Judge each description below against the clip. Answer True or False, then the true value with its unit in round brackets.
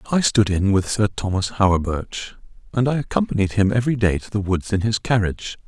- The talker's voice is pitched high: False (105 Hz)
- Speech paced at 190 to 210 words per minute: True (200 wpm)